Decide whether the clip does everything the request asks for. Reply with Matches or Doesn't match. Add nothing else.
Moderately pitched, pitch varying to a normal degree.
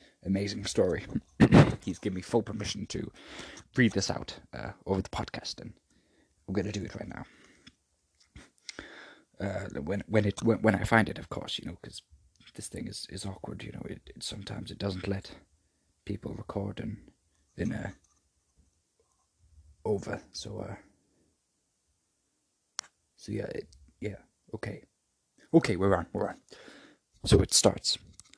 Doesn't match